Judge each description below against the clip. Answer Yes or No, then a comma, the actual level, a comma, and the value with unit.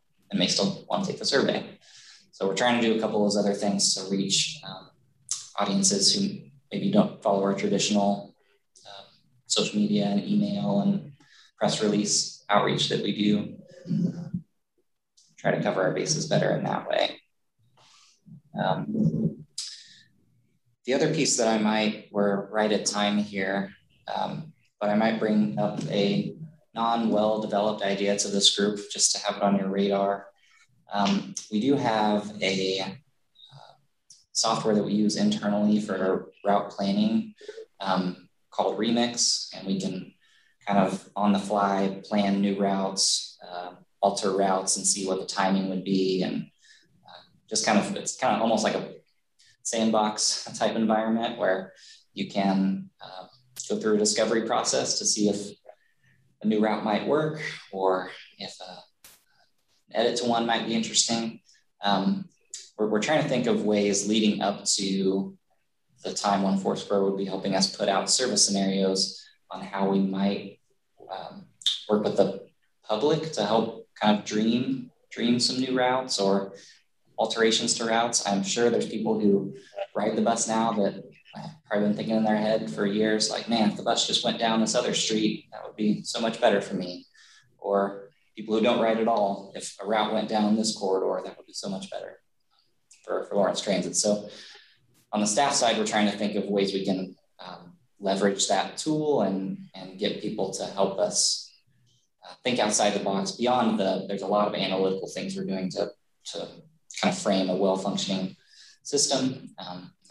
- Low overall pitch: Yes, low, 105 Hz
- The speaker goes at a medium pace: Yes, average, 175 wpm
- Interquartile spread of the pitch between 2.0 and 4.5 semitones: Yes, average, 2.9 semitones